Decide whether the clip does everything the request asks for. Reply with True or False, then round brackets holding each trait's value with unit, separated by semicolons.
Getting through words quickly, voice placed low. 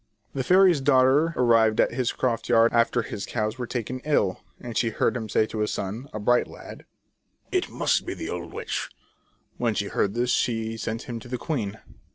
True (210 wpm; 120 Hz)